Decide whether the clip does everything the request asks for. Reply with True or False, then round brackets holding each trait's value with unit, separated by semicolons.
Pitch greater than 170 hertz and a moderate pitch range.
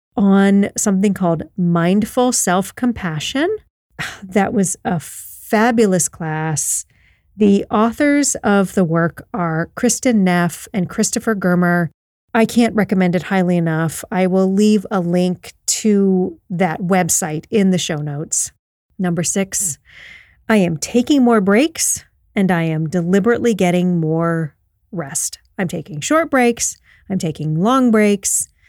True (190 Hz; 4.3 semitones)